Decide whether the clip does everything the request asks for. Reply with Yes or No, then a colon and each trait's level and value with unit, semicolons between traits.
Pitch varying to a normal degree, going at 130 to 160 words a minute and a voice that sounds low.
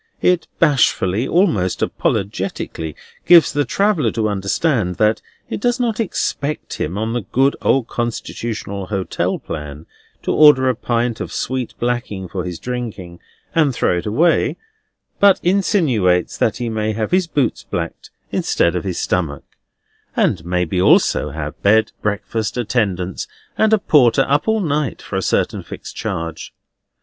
No: wide, 7.5 semitones; average, 150 wpm; low, 115 Hz